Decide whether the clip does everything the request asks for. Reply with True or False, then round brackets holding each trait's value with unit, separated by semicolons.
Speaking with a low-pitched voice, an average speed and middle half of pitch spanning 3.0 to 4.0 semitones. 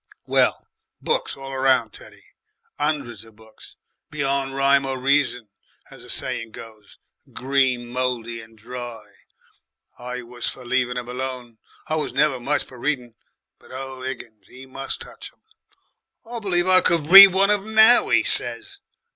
True (130 Hz; 155 wpm; 3.4 semitones)